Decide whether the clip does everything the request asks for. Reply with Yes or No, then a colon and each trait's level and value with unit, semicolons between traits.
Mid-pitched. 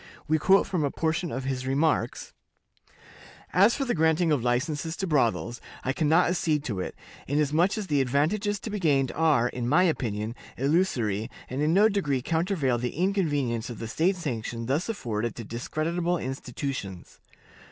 Yes: medium, 150 Hz